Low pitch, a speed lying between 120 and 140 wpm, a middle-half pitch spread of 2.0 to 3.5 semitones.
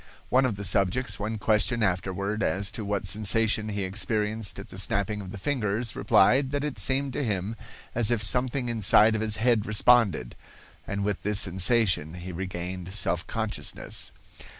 No: low, 105 Hz; average, 170 wpm; average, 2.9 semitones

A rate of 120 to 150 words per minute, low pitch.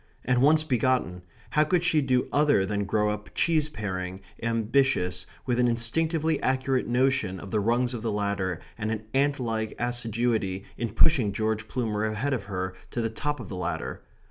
No: average, 180 wpm; low, 115 Hz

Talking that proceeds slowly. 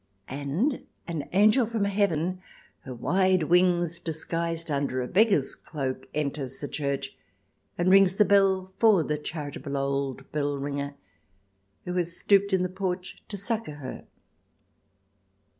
Yes: slow, 130 wpm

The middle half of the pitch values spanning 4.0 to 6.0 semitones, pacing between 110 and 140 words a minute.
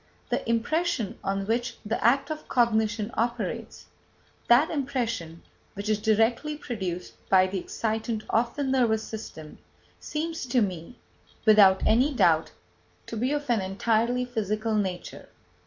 No: average, 3.3 semitones; slow, 135 wpm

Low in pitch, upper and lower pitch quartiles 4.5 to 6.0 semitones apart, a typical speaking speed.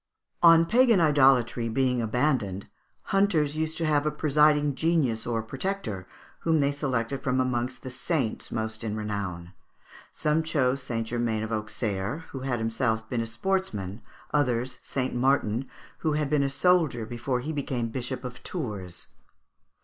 Yes: low, 130 Hz; average, 4.9 semitones; average, 150 wpm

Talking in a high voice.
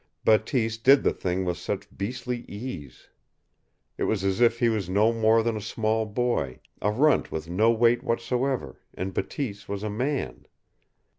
No: low, 110 Hz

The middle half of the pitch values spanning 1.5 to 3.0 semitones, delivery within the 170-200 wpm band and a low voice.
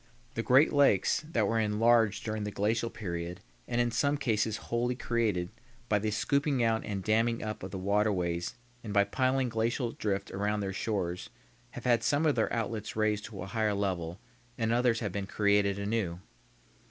Yes: average, 2.7 semitones; average, 180 wpm; low, 110 Hz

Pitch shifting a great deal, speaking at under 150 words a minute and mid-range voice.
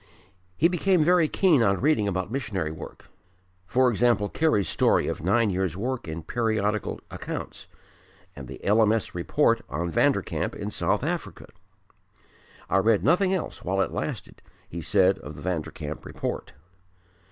No: wide, 5.8 semitones; average, 140 wpm; low, 105 Hz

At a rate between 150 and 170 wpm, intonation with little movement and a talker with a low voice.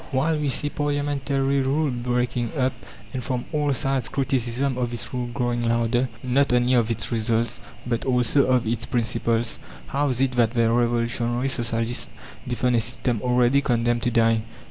Yes: average, 165 wpm; narrow, 2.2 semitones; low, 125 Hz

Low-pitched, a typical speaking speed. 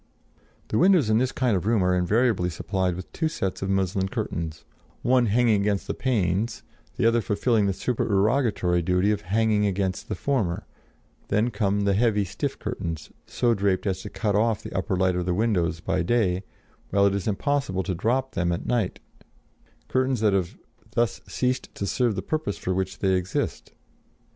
Yes: low, 100 Hz; average, 180 wpm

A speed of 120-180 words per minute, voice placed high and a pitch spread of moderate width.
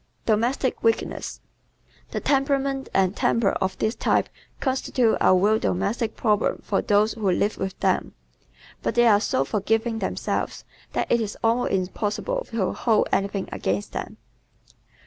Yes: average, 145 wpm; high, 220 Hz; average, 3.3 semitones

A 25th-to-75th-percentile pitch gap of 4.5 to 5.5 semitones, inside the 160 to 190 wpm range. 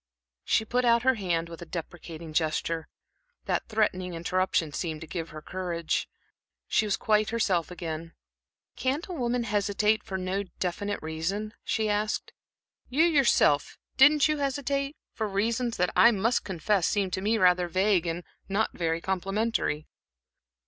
No: average, 5.0 semitones; average, 150 wpm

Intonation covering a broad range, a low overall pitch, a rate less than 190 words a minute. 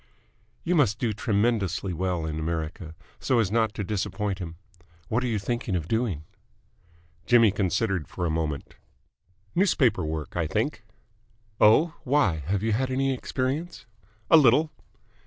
Yes: wide, 5.9 semitones; low, 105 Hz; average, 145 wpm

